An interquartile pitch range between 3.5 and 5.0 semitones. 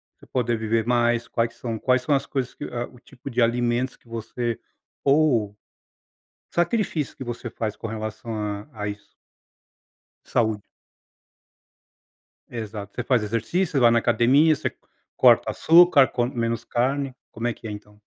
No: average, 2.7 semitones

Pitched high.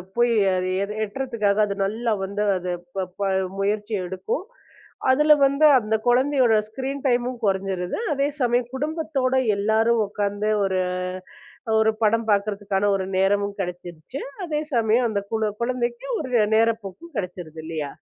Yes: high, 220 Hz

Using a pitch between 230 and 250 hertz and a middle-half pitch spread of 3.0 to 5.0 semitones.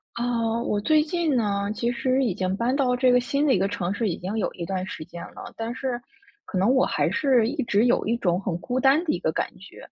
Yes: high, 235 Hz; average, 4.6 semitones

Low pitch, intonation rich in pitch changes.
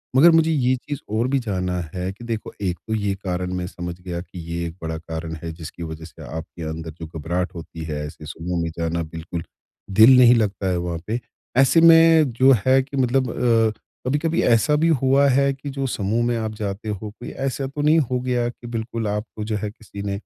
Yes: low, 110 Hz; wide, 7.0 semitones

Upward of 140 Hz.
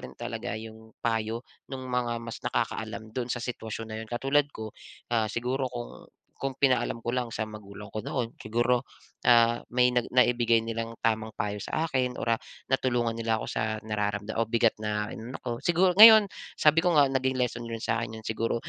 No: low, 115 Hz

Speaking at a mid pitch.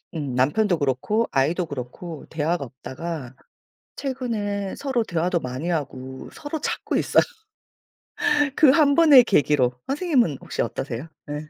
Yes: medium, 165 Hz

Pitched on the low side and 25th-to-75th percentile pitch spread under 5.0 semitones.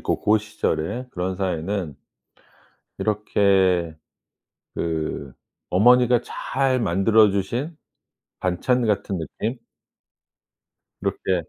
Yes: low, 100 Hz; average, 4.5 semitones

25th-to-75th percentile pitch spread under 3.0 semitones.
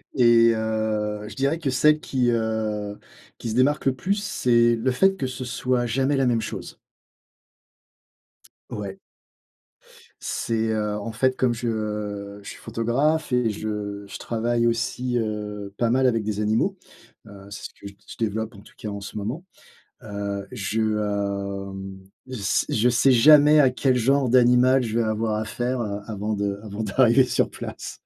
No: average, 3.3 semitones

